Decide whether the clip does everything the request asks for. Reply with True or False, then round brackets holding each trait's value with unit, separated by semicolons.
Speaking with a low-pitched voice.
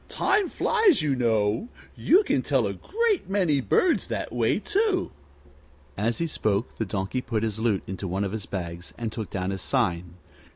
True (115 Hz)